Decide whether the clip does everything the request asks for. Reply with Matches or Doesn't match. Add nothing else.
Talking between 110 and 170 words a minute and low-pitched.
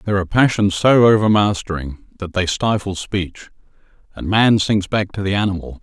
Matches